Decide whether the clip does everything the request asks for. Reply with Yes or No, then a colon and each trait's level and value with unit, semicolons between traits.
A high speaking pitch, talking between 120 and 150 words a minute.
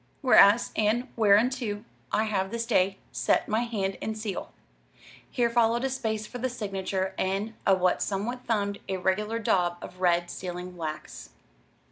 Yes: high, 210 Hz; average, 145 wpm